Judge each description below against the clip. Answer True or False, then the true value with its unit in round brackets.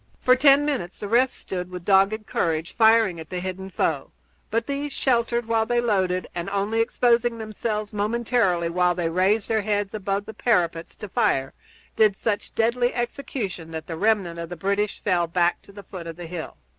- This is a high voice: True (205 Hz)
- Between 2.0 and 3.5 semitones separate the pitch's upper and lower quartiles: False (4.4 semitones)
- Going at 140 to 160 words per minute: False (190 wpm)